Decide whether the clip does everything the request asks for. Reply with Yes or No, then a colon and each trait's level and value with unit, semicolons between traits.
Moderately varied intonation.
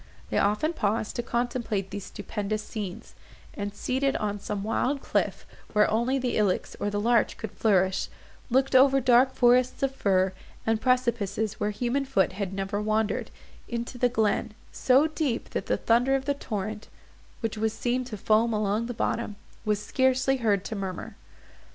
Yes: average, 3.6 semitones